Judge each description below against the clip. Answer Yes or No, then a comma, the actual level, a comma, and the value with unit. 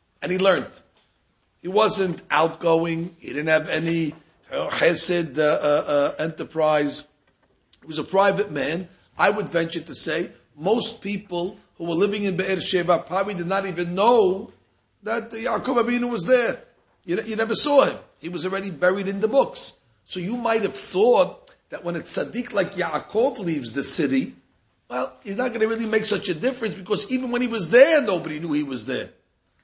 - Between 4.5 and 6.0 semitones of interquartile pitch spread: Yes, wide, 5.5 semitones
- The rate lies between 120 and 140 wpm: No, average, 180 wpm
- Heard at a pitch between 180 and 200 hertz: Yes, high, 190 Hz